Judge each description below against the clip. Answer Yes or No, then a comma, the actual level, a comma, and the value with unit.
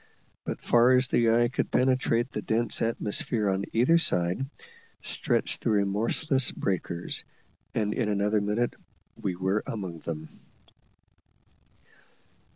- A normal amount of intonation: Yes, average, 3.5 semitones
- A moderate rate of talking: No, slow, 120 wpm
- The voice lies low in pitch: Yes, low, 110 Hz